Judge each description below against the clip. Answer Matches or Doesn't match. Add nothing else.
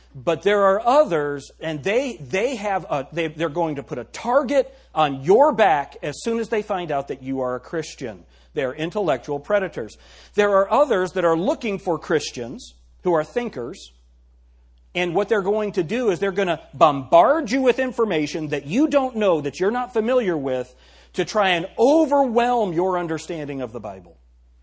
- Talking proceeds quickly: Doesn't match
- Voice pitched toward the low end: Doesn't match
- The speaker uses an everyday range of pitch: Doesn't match